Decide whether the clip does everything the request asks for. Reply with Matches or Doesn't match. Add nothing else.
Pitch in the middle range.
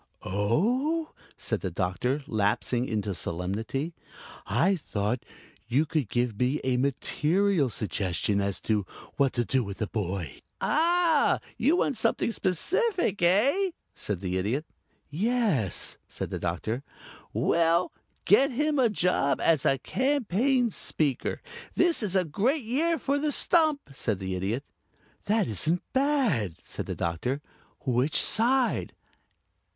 Matches